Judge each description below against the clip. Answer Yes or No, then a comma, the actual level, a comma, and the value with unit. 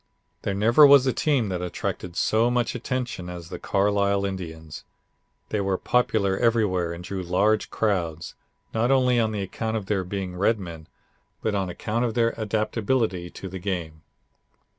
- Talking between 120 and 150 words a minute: No, average, 160 wpm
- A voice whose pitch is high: No, low, 100 Hz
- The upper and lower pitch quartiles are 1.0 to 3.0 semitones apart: No, average, 4.0 semitones